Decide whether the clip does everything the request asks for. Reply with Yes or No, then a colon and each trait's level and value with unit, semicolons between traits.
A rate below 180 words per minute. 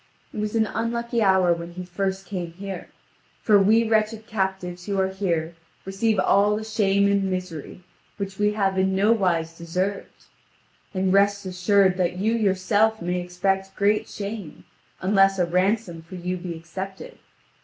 Yes: average, 160 wpm